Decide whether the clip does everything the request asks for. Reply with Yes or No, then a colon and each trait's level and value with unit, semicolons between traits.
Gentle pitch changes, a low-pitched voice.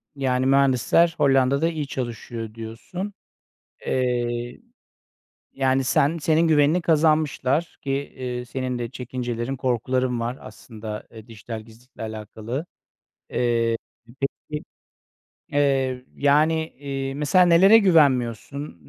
No: average, 3.7 semitones; low, 130 Hz